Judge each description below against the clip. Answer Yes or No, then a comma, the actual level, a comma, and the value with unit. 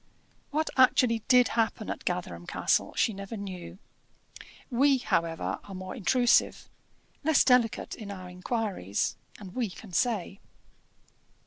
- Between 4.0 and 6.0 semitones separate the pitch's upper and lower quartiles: Yes, average, 5.3 semitones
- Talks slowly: Yes, slow, 125 wpm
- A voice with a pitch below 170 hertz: No, high, 215 Hz